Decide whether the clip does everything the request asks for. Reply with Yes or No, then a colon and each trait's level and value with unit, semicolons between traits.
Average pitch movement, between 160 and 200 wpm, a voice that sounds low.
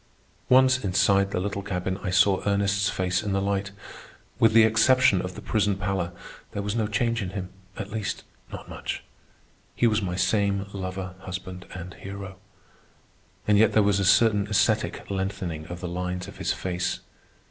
No: narrow, 2.0 semitones; average, 170 wpm; low, 100 Hz